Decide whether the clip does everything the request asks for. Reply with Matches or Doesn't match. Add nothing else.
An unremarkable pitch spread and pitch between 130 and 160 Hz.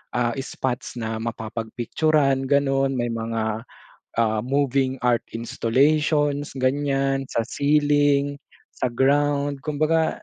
Matches